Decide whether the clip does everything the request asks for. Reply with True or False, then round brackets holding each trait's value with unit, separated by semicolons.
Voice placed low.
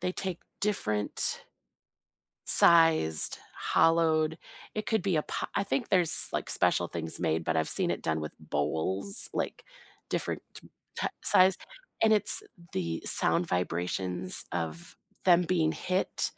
False (155 Hz)